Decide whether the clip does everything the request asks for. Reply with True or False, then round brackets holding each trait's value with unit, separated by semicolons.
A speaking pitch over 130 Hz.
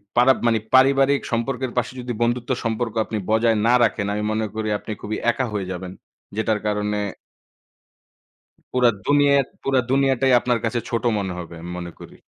False (115 Hz)